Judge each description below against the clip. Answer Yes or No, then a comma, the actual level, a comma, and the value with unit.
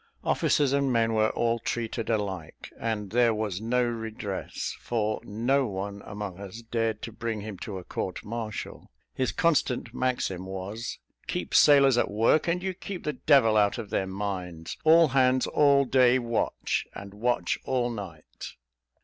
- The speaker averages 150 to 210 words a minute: Yes, average, 160 wpm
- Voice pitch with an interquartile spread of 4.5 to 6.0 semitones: No, average, 3.8 semitones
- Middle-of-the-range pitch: No, low, 115 Hz